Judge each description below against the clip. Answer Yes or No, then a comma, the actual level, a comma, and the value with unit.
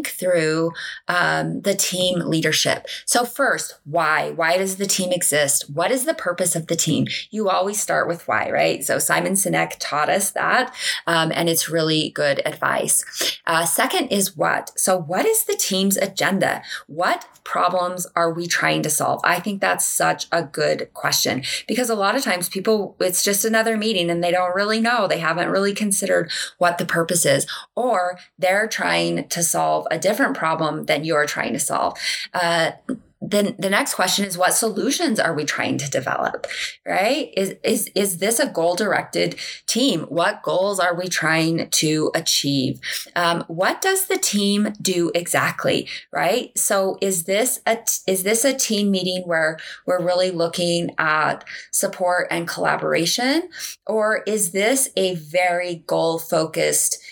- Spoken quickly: No, average, 165 wpm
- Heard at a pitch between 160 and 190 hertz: Yes, medium, 185 Hz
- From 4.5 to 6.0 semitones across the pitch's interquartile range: No, average, 3.6 semitones